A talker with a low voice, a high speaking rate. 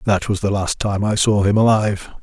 Yes: low, 100 Hz; fast, 240 wpm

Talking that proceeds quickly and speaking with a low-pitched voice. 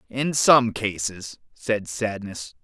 No: slow, 115 wpm; low, 110 Hz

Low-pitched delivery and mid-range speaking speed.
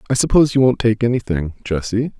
Yes: low, 115 Hz; average, 165 wpm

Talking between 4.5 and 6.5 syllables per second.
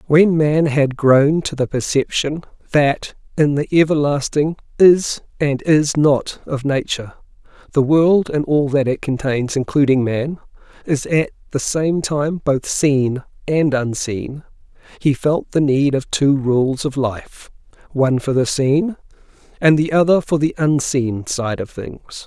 No: 3.9 syllables/s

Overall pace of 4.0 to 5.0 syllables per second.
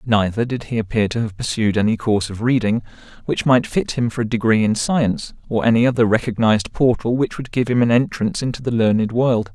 No: 6.0 syllables/s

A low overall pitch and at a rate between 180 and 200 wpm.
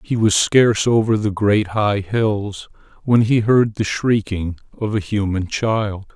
No: low, 105 Hz; average, 165 wpm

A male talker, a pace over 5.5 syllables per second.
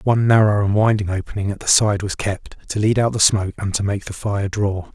Yes: male; 5.7 syllables/s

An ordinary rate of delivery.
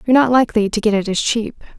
No: fast, 270 wpm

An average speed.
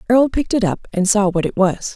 No: fast, 275 wpm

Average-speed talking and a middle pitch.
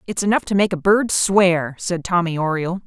No: fast, 210 wpm; medium, 180 Hz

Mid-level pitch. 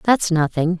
Yes: medium, 170 Hz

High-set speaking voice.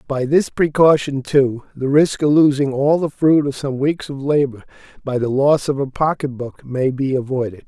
No: medium, 140 Hz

